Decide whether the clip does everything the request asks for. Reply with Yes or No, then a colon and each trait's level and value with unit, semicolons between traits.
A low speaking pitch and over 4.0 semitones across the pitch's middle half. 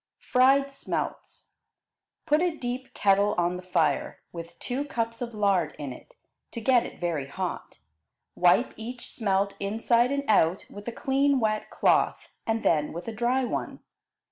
No: high, 225 Hz; wide, 5.6 semitones